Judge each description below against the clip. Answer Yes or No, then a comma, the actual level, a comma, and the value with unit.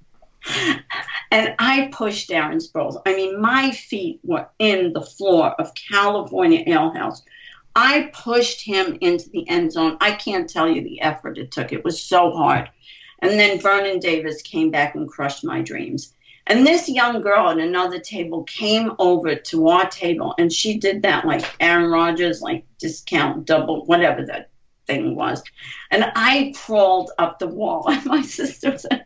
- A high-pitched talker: Yes, high, 210 Hz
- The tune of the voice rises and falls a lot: Yes, wide, 8.3 semitones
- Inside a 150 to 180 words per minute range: Yes, average, 170 wpm